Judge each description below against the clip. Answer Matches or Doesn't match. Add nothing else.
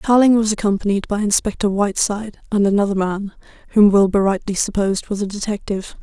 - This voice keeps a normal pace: Matches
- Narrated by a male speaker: Doesn't match